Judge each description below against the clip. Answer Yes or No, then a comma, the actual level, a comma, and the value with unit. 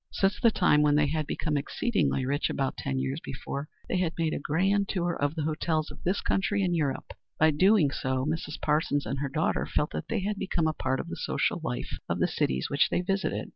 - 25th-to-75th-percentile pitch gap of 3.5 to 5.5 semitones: Yes, average, 4.2 semitones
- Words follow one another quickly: Yes, fast, 225 wpm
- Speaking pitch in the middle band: Yes, medium, 155 Hz